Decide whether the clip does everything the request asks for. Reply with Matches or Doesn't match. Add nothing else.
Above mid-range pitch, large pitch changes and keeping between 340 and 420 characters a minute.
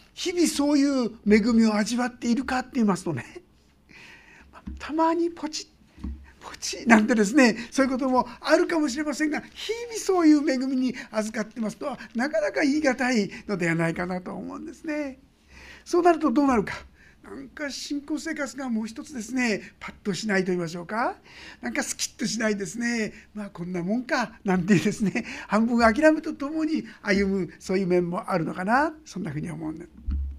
Matches